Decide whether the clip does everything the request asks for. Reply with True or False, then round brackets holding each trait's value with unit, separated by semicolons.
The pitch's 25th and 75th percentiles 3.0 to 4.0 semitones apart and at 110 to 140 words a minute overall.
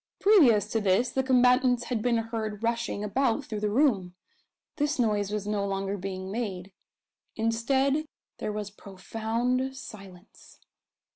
True (3.6 semitones; 135 wpm)